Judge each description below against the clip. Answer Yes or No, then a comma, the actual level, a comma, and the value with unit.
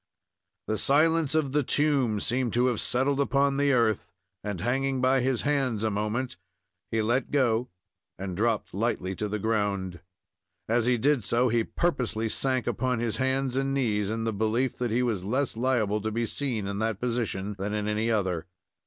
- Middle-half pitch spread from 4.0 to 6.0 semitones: No, average, 3.6 semitones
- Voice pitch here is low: Yes, low, 120 Hz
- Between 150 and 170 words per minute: No, average, 185 wpm